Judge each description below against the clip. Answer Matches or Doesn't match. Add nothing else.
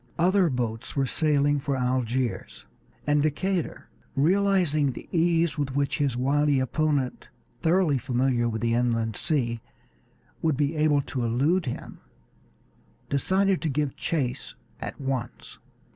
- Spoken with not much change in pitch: Doesn't match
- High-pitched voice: Doesn't match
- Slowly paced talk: Matches